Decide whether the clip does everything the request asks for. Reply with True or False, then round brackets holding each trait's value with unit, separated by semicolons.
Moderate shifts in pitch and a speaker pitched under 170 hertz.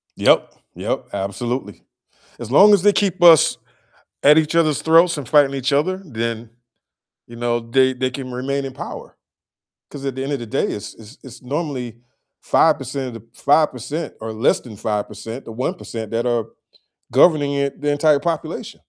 True (4.2 semitones; 135 Hz)